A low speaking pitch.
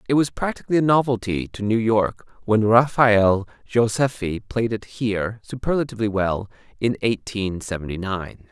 Yes: low, 110 Hz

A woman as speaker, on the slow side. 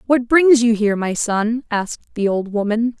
No: female; average, 200 wpm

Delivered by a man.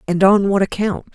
No: female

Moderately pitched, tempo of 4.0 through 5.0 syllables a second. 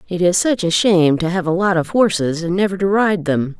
No: medium, 180 Hz; 5.5 syllables/s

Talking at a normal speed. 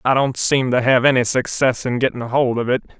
No: fast, 240 wpm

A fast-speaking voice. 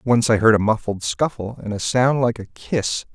Yes: fast, 230 wpm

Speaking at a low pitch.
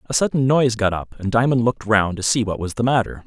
Yes: low, 115 Hz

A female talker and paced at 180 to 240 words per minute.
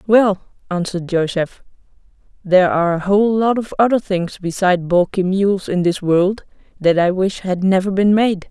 No: female; average, 170 wpm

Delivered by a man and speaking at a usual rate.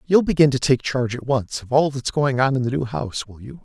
No: male; fast, 295 wpm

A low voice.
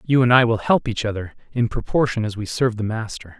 Yes: low, 115 Hz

